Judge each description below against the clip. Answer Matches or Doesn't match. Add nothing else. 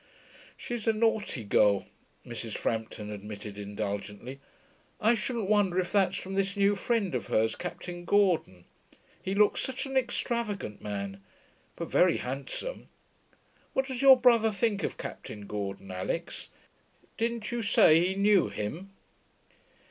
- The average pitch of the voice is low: Doesn't match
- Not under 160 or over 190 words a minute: Doesn't match